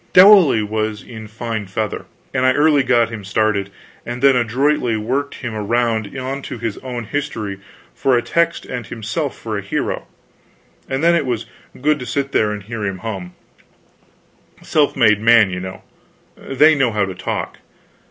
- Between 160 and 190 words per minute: Yes, average, 170 wpm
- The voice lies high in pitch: No, low, 115 Hz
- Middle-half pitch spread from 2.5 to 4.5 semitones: Yes, average, 4.1 semitones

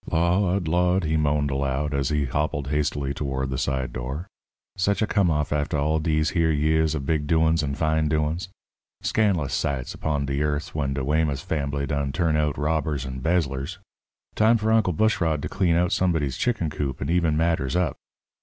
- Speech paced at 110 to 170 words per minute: No, average, 185 wpm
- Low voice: Yes, very low, 75 Hz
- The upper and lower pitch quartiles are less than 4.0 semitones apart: Yes, average, 3.0 semitones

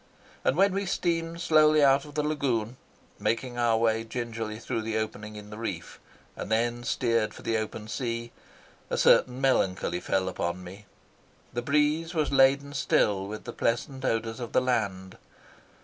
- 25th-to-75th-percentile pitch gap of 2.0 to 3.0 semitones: No, average, 4.4 semitones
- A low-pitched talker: Yes, low, 115 Hz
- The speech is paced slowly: No, average, 165 wpm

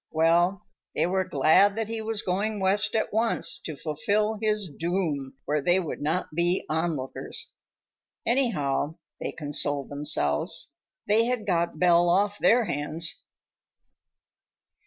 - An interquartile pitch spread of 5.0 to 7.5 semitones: Yes, wide, 5.4 semitones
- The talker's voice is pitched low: No, medium, 175 Hz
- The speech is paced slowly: Yes, slow, 130 wpm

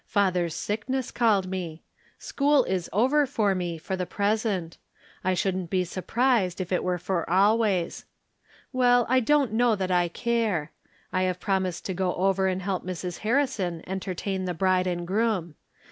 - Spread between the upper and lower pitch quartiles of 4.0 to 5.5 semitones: No, average, 3.6 semitones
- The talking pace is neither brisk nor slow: Yes, average, 160 wpm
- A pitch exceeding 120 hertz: Yes, high, 190 Hz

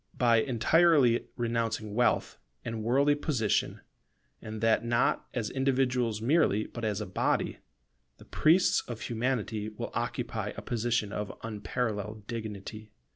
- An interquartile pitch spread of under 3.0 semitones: Yes, narrow, 2.6 semitones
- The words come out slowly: Yes, slow, 130 wpm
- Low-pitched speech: Yes, low, 115 Hz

